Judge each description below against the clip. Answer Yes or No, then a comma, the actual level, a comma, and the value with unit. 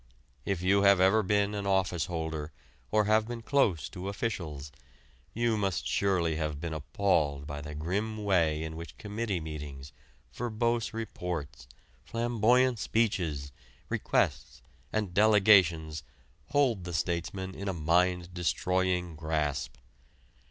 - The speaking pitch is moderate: No, very low, 90 Hz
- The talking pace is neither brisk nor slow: No, slow, 125 wpm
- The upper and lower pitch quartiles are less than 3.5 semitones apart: No, average, 4.9 semitones